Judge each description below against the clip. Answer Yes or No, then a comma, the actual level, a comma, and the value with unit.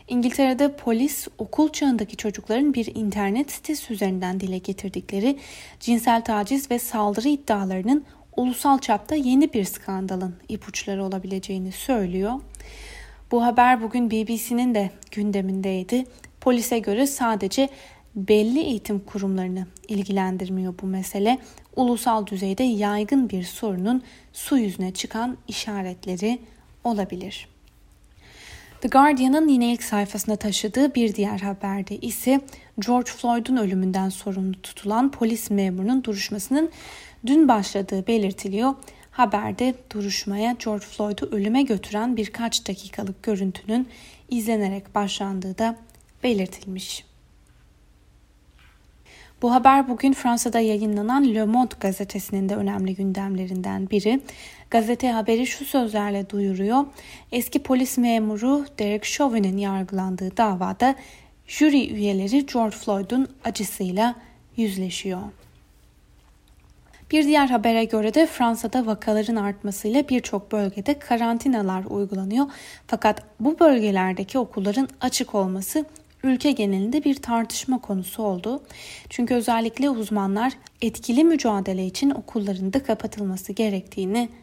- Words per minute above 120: No, average, 105 wpm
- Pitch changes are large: No, average, 4.1 semitones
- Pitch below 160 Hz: No, high, 220 Hz